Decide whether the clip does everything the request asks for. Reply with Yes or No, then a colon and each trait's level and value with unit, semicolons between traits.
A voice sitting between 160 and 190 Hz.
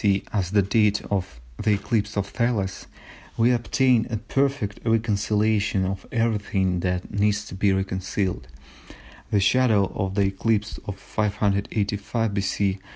No: low, 100 Hz